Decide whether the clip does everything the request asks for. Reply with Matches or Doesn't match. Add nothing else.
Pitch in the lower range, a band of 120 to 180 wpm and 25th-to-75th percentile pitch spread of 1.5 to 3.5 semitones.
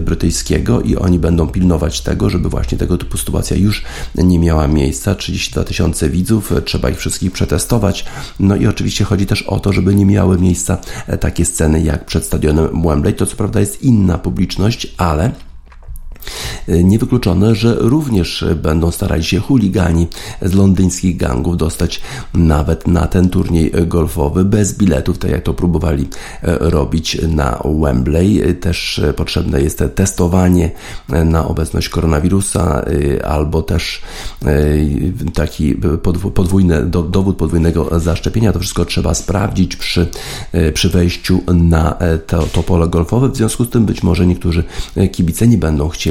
Matches